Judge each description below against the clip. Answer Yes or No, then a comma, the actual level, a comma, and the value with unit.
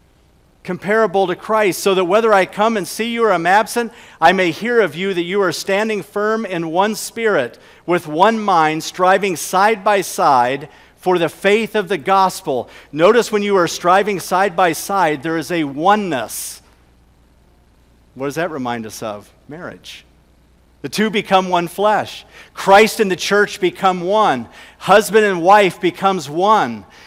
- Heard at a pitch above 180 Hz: Yes, high, 190 Hz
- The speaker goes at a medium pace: Yes, average, 165 wpm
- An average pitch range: Yes, average, 4.4 semitones